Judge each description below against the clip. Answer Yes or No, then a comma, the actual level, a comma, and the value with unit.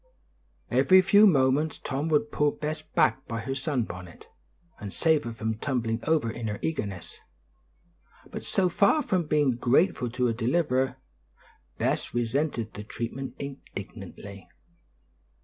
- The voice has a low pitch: Yes, low, 130 Hz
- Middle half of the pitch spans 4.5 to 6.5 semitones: Yes, average, 5.1 semitones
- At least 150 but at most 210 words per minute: No, slow, 135 wpm